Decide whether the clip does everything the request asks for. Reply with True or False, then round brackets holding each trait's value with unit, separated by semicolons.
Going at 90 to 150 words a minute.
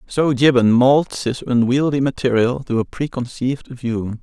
True (140 wpm)